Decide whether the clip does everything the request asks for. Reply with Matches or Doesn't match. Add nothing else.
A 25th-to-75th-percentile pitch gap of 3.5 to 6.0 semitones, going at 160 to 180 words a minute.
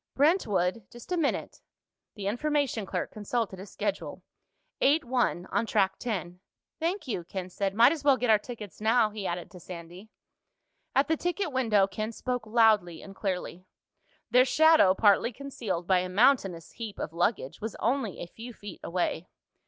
Matches